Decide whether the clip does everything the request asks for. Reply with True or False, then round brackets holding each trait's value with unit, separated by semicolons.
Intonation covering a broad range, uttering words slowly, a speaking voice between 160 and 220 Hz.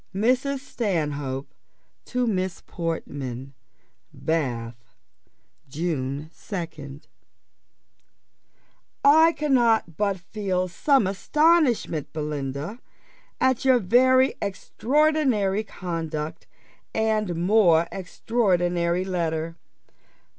True (6.9 semitones; 70 wpm; 185 Hz)